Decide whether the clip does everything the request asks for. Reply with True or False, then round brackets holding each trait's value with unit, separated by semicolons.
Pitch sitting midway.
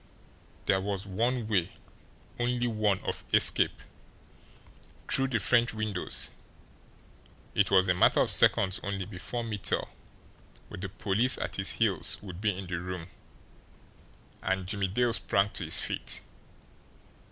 False (100 Hz)